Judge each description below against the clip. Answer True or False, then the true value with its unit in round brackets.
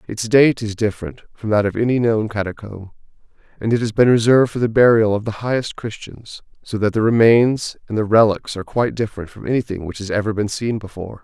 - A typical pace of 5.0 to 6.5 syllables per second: True (6.1 syllables/s)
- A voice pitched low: True (110 Hz)